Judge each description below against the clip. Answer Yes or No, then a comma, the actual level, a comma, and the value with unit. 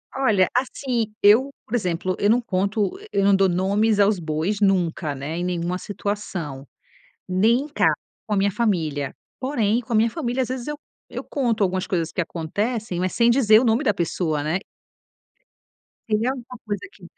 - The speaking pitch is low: No, high, 205 Hz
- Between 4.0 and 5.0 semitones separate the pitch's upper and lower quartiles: Yes, average, 4.6 semitones